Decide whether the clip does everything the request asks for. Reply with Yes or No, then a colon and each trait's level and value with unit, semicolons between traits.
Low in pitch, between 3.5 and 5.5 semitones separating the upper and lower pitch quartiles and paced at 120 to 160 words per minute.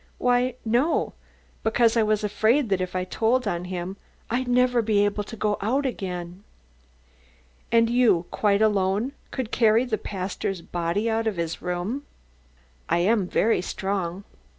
No: high, 210 Hz; average, 4.1 semitones; average, 150 wpm